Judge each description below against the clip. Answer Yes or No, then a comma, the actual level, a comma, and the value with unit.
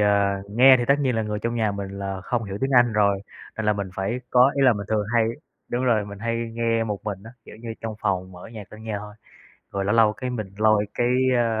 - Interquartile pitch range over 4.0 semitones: No, narrow, 2.6 semitones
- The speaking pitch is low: Yes, low, 110 Hz